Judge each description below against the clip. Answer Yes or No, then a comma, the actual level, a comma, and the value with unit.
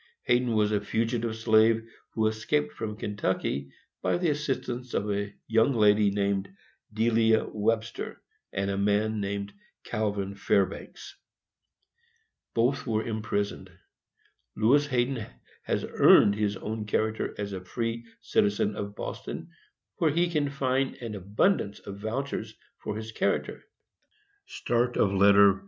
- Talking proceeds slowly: Yes, slow, 120 wpm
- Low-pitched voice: Yes, low, 110 Hz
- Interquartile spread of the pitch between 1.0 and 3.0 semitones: Yes, narrow, 2.6 semitones